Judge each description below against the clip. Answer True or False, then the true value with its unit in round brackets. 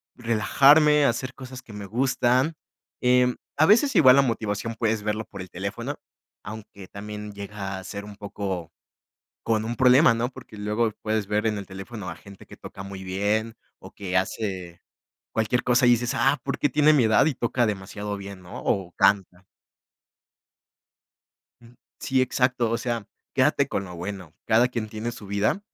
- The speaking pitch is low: True (110 Hz)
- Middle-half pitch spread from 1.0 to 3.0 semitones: False (3.8 semitones)